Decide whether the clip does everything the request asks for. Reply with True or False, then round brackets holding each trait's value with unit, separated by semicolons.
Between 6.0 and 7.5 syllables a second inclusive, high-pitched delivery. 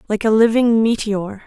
False (4.7 syllables/s; 220 Hz)